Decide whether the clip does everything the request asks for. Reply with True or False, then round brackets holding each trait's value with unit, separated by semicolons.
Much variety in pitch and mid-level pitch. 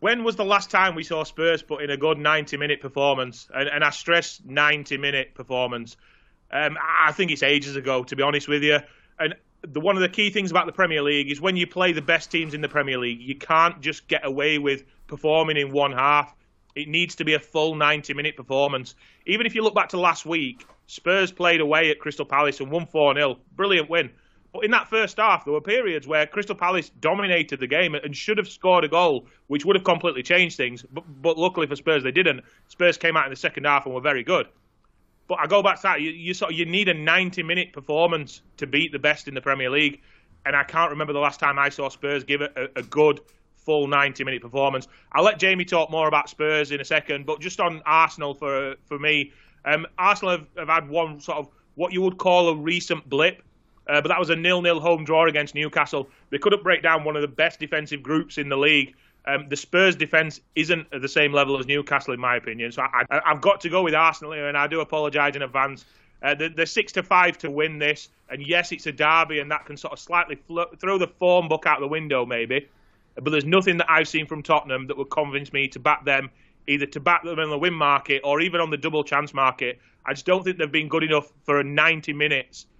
False (3.1 semitones; 150 Hz)